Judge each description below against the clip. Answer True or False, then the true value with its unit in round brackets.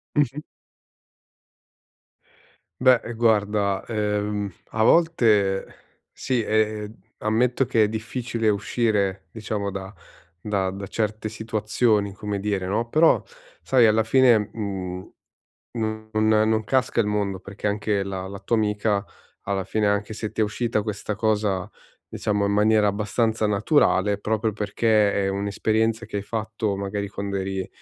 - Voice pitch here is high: False (105 Hz)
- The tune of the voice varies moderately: False (1.7 semitones)